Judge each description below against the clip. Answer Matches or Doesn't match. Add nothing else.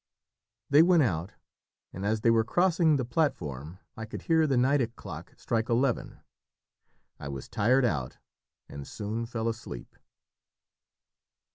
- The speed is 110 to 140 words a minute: Matches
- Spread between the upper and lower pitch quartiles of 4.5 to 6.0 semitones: Matches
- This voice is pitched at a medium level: Doesn't match